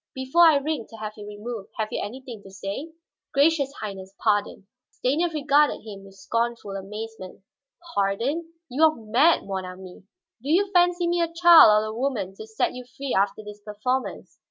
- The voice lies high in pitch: Yes, high, 230 Hz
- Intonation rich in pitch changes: Yes, wide, 6.4 semitones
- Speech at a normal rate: Yes, average, 180 wpm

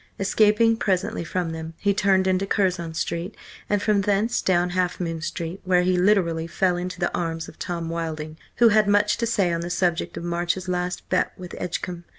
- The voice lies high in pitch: No, medium, 180 Hz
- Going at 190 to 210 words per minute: Yes, average, 195 wpm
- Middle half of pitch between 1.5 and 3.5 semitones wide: Yes, average, 2.7 semitones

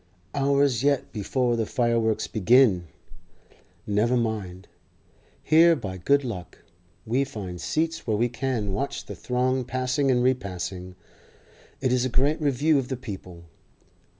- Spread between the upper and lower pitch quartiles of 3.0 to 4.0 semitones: No, average, 4.5 semitones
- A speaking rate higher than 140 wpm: No, slow, 135 wpm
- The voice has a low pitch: Yes, low, 125 Hz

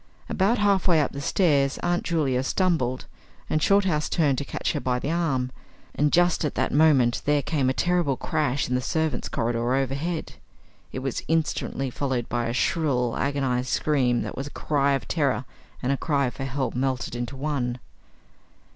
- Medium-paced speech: Yes, average, 180 wpm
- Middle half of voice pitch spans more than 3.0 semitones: Yes, average, 3.8 semitones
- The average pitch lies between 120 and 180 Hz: Yes, medium, 140 Hz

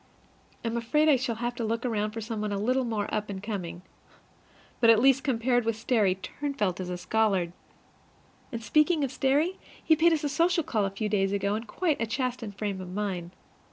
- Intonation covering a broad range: No, average, 4.6 semitones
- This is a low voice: No, high, 225 Hz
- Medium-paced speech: No, fast, 215 wpm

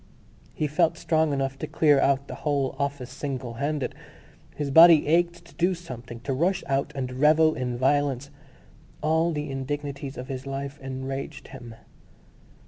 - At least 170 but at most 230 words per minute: No, average, 150 wpm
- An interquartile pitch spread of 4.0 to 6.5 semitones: No, narrow, 2.5 semitones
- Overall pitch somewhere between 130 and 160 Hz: Yes, medium, 140 Hz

